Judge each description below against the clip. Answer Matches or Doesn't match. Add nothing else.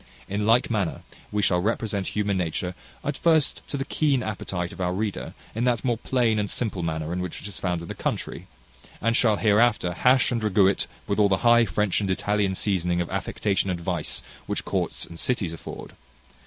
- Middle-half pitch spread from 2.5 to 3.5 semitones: Doesn't match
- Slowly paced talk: Doesn't match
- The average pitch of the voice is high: Doesn't match